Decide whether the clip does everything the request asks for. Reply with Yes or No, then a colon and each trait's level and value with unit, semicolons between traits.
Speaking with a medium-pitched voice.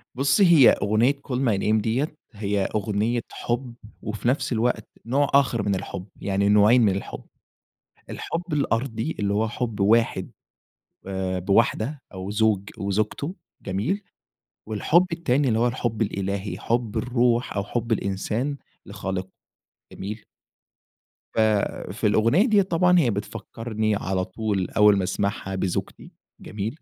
No: low, 110 Hz